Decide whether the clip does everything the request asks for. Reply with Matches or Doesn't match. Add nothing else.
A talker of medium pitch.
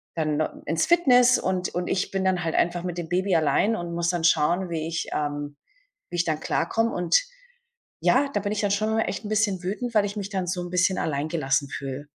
Matches